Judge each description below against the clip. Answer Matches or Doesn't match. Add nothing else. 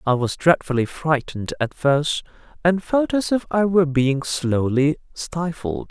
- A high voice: Doesn't match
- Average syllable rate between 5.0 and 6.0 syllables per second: Doesn't match